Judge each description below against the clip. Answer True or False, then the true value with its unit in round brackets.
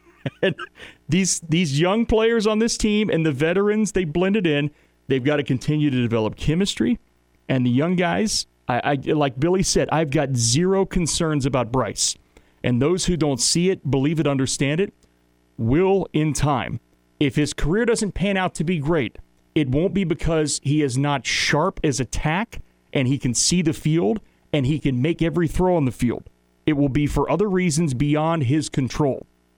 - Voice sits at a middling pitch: True (150 Hz)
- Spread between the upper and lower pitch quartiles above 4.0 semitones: True (5.1 semitones)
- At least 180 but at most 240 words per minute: True (185 wpm)